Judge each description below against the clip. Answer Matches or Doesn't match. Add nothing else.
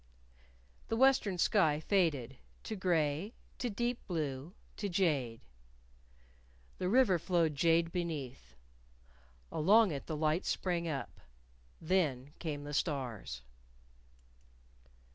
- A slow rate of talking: Matches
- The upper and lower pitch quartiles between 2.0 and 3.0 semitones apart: Doesn't match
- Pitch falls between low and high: Matches